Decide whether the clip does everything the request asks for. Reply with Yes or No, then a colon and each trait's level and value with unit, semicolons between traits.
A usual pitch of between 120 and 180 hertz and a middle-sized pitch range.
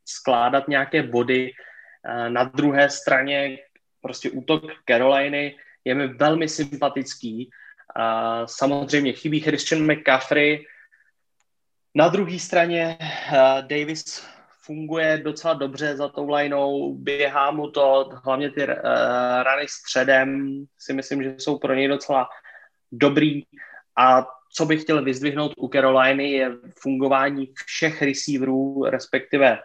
No: medium, 140 Hz; narrow, 2.0 semitones